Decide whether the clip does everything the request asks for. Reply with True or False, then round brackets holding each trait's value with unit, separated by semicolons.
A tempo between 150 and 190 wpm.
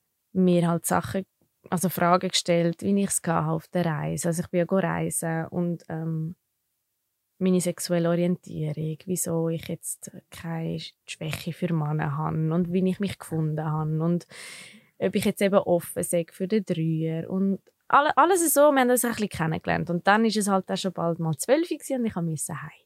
True (185 wpm)